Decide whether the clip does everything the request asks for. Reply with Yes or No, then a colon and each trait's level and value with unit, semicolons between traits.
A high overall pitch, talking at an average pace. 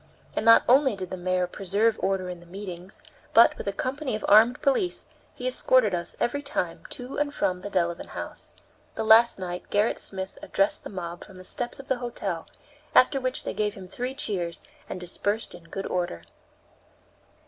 Yes: high, 200 Hz; average, 190 wpm